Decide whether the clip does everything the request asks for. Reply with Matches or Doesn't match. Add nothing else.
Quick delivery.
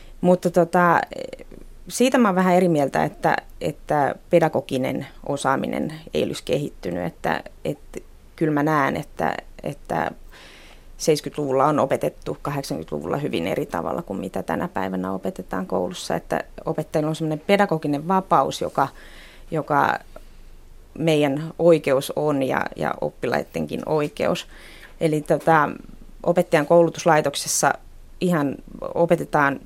Doesn't match